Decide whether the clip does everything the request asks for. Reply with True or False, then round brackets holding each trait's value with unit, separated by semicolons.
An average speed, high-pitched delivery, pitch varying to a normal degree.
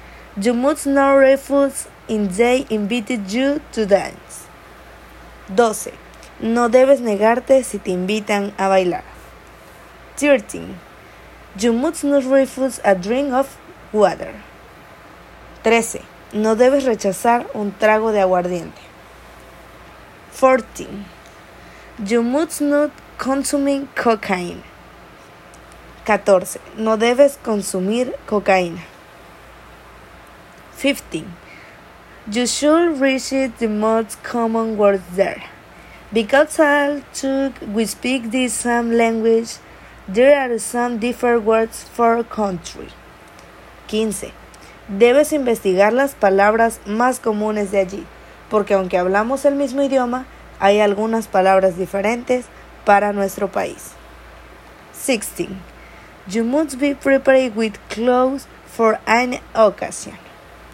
False (100 wpm; 230 Hz; 4.3 semitones)